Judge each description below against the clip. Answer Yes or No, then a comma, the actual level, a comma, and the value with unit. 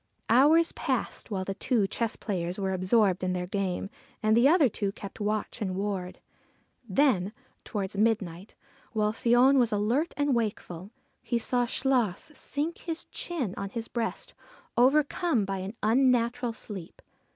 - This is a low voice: No, high, 220 Hz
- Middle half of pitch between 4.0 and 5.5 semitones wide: Yes, average, 4.4 semitones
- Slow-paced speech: No, average, 150 wpm